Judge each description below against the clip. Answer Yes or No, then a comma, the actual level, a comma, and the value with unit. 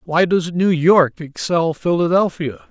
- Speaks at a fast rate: No, slow, 135 wpm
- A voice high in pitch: No, medium, 170 Hz